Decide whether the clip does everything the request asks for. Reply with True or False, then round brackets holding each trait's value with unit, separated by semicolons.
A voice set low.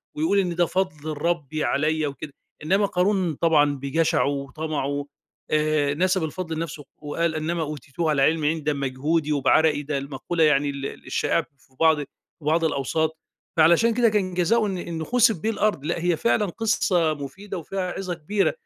False (160 Hz)